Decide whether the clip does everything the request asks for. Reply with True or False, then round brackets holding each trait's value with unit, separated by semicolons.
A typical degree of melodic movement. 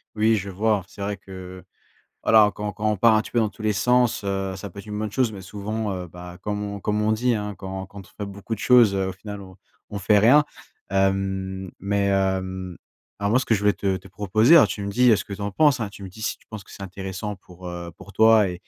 False (2.1 semitones)